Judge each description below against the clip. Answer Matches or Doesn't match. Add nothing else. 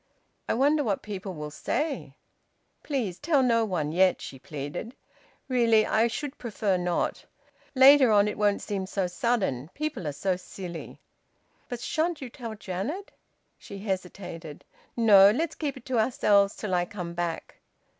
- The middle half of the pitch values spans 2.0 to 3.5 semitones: Doesn't match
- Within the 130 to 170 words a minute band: Matches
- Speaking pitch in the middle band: Doesn't match